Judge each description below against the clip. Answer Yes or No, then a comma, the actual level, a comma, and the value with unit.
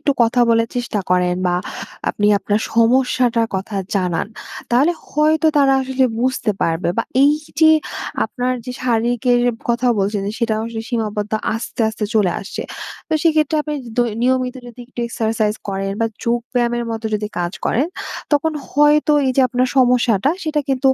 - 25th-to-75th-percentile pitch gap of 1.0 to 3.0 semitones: No, average, 3.4 semitones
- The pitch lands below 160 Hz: No, high, 240 Hz